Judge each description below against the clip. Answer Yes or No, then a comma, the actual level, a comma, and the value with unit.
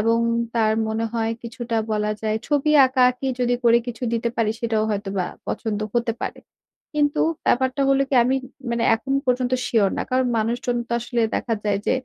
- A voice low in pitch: No, high, 235 Hz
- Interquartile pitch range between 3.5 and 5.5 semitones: No, narrow, 2.4 semitones